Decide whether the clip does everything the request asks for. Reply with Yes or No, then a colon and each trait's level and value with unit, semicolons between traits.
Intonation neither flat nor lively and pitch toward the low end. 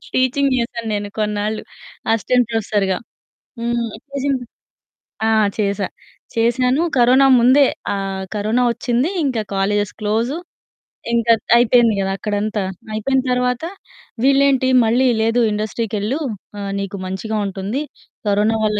No: average, 3.3 semitones; high, 225 Hz